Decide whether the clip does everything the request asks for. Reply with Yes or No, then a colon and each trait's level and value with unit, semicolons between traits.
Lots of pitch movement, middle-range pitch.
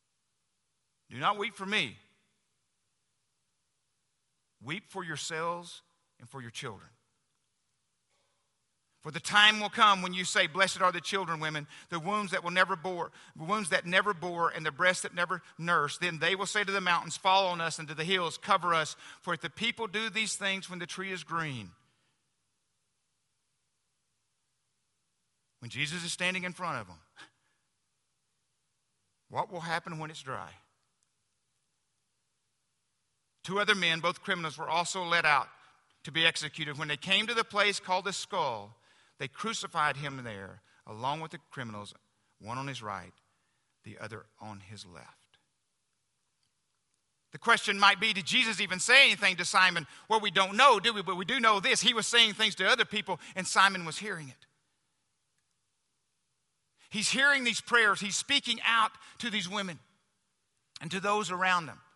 Yes: wide, 5.7 semitones; medium, 175 Hz